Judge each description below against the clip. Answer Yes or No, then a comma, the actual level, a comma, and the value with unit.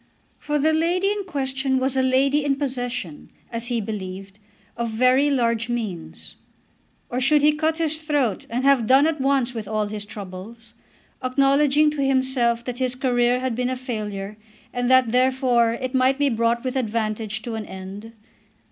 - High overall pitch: Yes, very high, 250 Hz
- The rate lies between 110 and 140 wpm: No, average, 175 wpm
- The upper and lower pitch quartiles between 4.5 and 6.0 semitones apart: No, average, 3.4 semitones